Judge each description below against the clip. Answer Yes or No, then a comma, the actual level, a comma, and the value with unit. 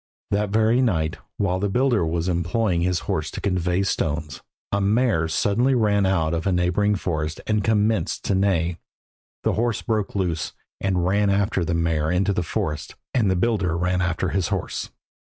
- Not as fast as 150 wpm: No, average, 175 wpm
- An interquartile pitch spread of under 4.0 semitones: Yes, average, 3.5 semitones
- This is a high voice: No, very low, 95 Hz